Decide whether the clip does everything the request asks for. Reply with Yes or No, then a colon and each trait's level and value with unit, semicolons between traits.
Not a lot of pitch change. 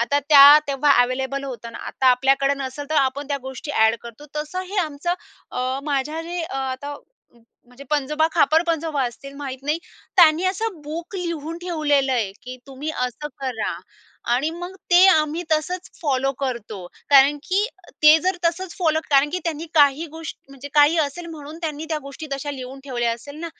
No: average, 3.4 semitones